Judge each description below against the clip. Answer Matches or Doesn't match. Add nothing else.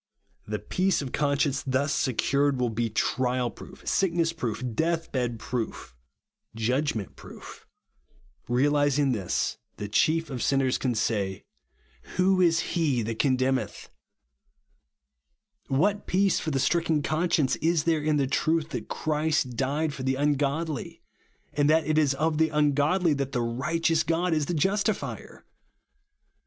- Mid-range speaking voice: Matches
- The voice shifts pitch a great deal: Doesn't match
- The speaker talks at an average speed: Matches